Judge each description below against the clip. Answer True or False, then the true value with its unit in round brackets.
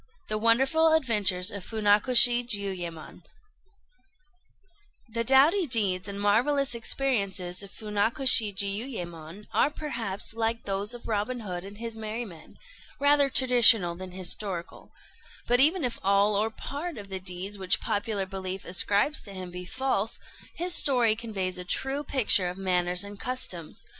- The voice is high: True (210 Hz)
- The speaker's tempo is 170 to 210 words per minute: False (145 wpm)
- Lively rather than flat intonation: False (4.5 semitones)